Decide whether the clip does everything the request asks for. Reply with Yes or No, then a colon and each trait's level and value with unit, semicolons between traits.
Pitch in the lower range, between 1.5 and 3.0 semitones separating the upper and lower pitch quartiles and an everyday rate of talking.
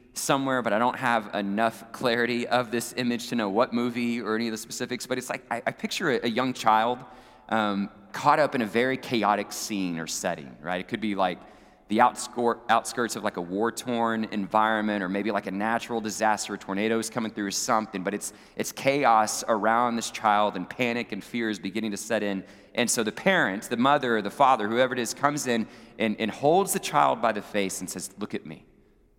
No: low, 110 Hz; average, 2.7 semitones; fast, 220 wpm